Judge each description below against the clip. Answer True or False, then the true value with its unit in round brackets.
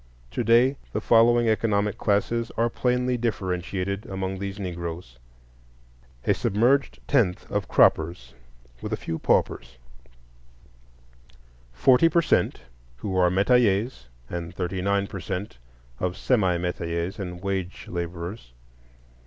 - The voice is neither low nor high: False (95 Hz)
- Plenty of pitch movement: False (4.6 semitones)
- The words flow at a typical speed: False (120 wpm)